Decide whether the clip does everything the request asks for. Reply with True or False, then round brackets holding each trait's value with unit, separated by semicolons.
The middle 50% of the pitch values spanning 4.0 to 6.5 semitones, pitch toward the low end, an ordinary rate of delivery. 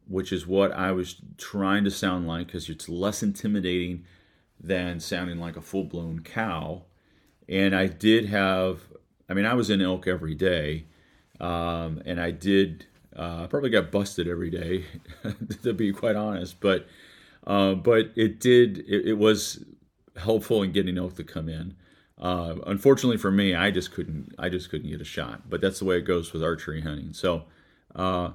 False (2.8 semitones; 90 Hz; 180 wpm)